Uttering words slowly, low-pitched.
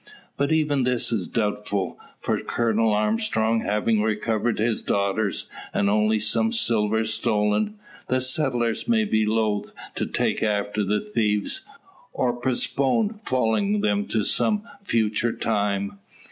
Yes: slow, 130 wpm; low, 110 Hz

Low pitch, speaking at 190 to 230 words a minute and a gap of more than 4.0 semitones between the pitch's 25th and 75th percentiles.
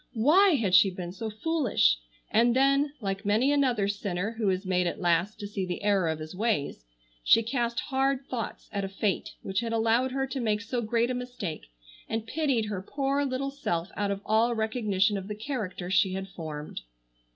No: high, 215 Hz; average, 195 wpm; average, 4.6 semitones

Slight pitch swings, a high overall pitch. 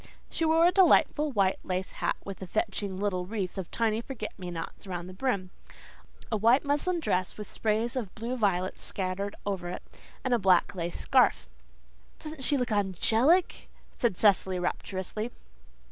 No: average, 5.0 semitones; high, 205 Hz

